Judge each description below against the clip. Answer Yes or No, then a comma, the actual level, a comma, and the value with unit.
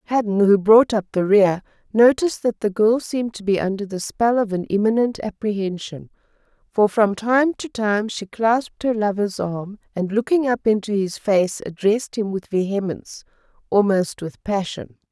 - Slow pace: No, average, 170 wpm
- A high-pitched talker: Yes, high, 210 Hz